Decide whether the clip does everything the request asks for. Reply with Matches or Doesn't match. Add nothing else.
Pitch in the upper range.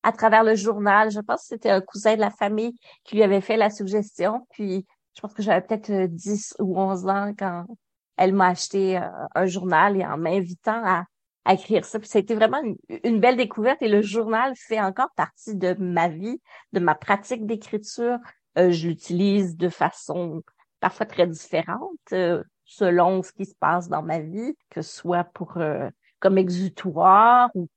Matches